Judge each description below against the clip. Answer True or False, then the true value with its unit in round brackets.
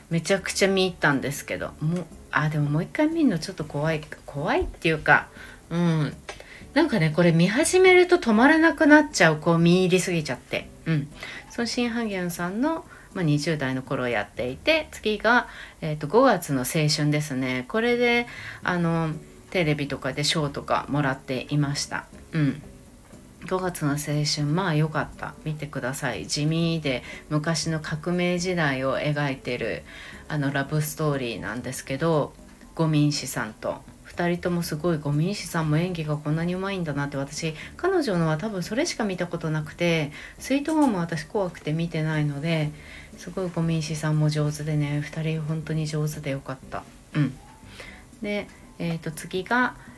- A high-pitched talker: False (160 Hz)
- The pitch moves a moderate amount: True (3.8 semitones)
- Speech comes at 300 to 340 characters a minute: True (335 characters per minute)